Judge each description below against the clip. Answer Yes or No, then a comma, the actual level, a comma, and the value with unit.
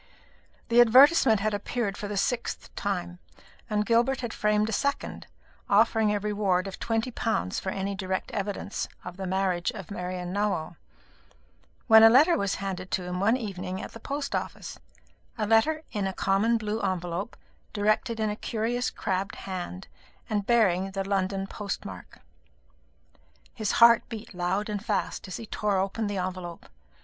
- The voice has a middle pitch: No, high, 205 Hz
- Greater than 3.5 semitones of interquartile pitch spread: No, average, 2.9 semitones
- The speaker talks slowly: No, average, 165 wpm